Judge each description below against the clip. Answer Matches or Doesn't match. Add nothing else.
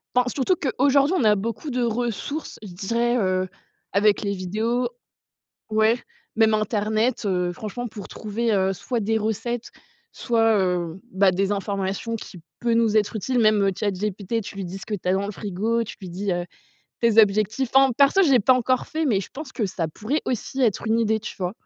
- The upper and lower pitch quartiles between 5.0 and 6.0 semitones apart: Doesn't match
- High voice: Matches